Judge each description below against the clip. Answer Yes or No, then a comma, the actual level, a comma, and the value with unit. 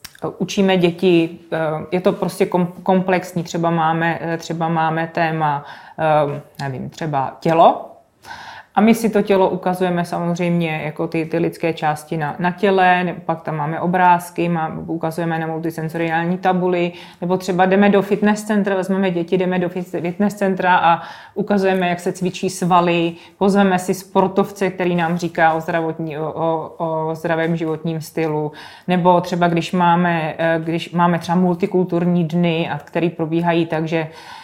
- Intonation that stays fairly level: Yes, narrow, 2.1 semitones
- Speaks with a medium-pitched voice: Yes, medium, 170 Hz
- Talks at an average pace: Yes, average, 145 wpm